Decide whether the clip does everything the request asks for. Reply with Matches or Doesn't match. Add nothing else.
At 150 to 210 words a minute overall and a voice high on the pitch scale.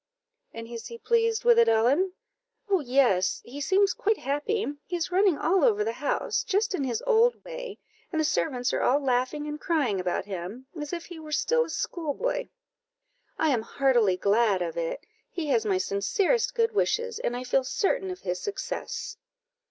Matches